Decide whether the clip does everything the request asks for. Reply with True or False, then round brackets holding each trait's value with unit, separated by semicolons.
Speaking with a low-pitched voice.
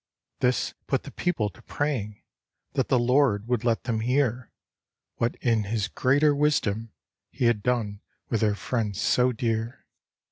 True (120 Hz)